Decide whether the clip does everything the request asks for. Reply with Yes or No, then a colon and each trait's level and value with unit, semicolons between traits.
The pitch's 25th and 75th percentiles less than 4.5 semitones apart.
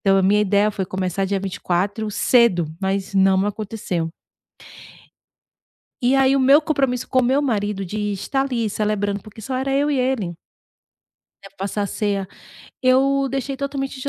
No: average, 5.2 semitones